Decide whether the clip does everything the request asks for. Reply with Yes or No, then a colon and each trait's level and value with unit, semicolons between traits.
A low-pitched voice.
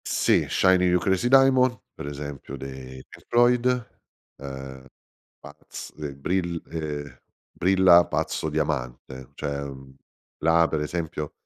Yes: very low, 75 Hz